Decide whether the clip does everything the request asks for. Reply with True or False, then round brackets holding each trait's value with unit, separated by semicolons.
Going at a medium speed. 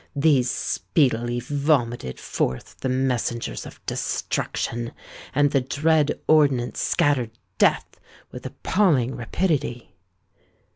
False (95 wpm)